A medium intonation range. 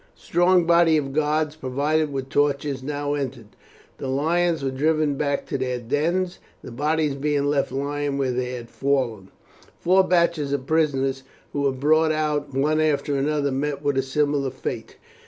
No: narrow, 2.3 semitones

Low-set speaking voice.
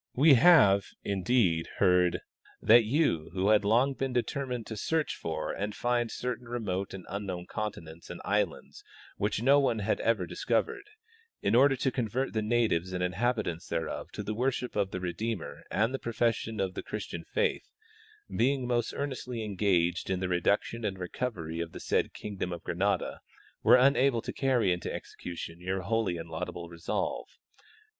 Yes: low, 105 Hz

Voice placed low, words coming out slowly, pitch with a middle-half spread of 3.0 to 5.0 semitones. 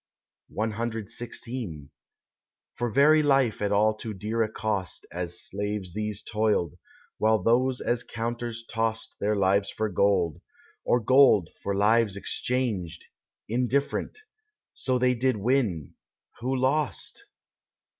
Yes: low, 110 Hz; slow, 115 wpm; average, 3.4 semitones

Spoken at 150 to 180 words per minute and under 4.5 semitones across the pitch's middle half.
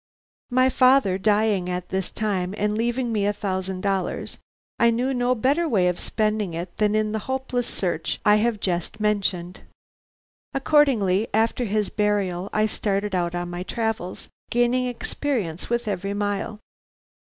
Yes: average, 155 wpm; average, 3.9 semitones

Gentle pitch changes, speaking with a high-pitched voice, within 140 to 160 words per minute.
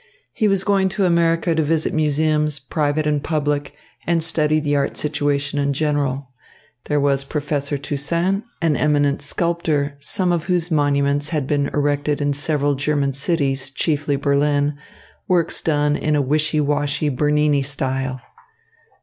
No: narrow, 1.8 semitones; medium, 145 Hz; average, 145 wpm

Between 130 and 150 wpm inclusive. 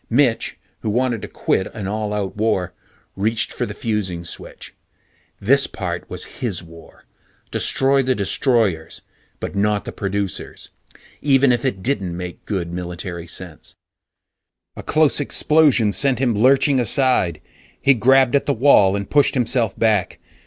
Yes: average, 145 wpm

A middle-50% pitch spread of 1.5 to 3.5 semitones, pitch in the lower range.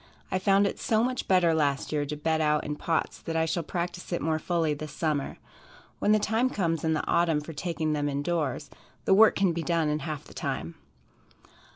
No: average, 3.0 semitones; medium, 160 Hz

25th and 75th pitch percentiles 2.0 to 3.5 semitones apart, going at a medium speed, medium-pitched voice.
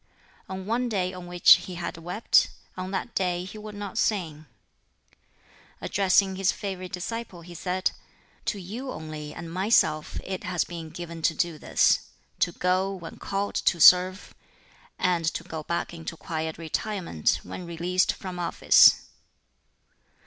Yes: narrow, 2.4 semitones; average, 150 wpm; medium, 180 Hz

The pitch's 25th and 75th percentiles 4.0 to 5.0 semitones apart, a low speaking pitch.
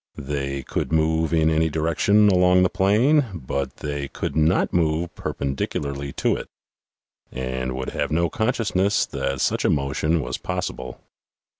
Yes: average, 4.7 semitones; very low, 80 Hz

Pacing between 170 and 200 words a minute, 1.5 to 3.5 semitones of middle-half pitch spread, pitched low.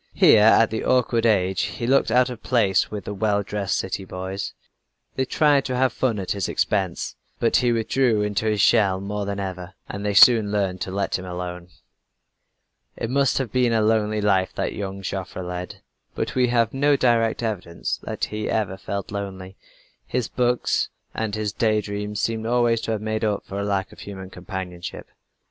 Yes: average, 190 wpm; average, 3.1 semitones; low, 105 Hz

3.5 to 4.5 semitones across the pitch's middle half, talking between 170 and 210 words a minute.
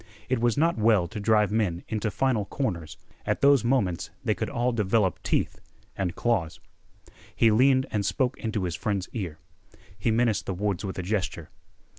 Yes: average, 3.9 semitones; average, 175 wpm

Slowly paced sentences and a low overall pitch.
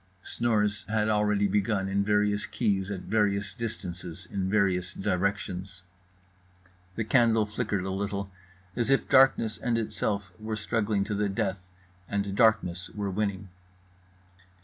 Yes: slow, 130 wpm; low, 100 Hz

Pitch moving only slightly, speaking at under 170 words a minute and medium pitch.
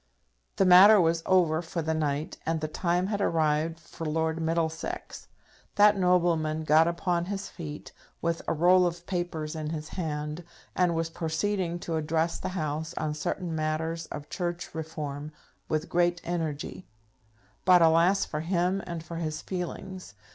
Yes: narrow, 2.1 semitones; average, 155 wpm; medium, 165 Hz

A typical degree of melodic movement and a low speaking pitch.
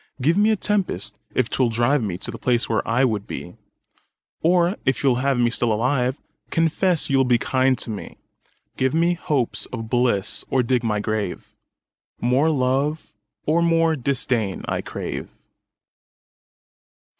Yes: average, 4.7 semitones; low, 130 Hz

